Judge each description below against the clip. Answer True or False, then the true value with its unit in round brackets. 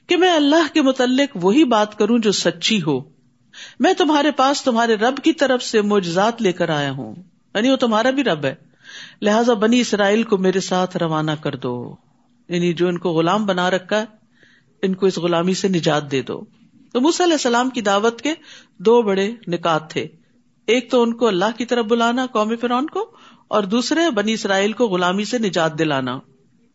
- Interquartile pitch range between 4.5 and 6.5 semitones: True (5.6 semitones)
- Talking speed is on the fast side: True (195 wpm)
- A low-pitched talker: False (215 Hz)